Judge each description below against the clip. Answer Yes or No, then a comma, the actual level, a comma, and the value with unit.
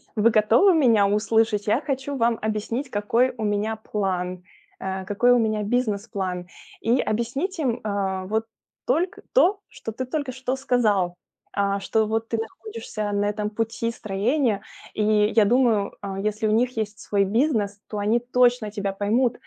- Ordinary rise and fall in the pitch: Yes, average, 3.2 semitones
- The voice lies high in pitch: Yes, high, 220 Hz